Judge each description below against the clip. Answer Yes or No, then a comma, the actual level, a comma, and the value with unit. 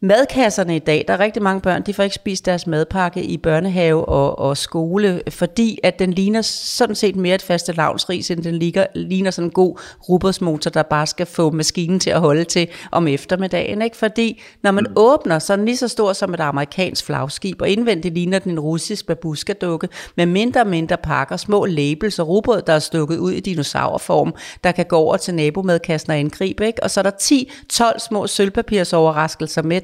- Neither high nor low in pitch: Yes, medium, 180 Hz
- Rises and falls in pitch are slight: No, average, 3.5 semitones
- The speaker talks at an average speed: Yes, average, 210 wpm